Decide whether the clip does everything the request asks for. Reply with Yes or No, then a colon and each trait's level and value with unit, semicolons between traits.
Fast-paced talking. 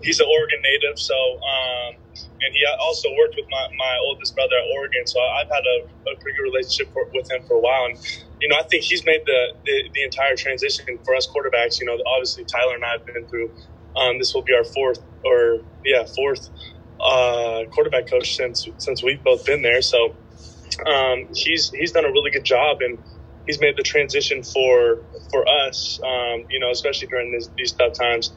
Yes: fast, 210 wpm